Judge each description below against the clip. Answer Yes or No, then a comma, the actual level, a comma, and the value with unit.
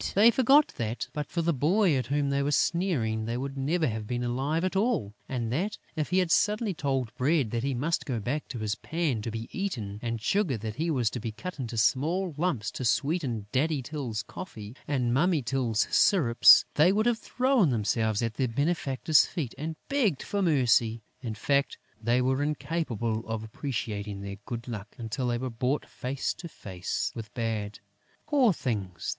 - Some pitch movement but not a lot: No, wide, 6.4 semitones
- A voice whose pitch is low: Yes, low, 130 Hz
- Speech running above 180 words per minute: Yes, average, 190 wpm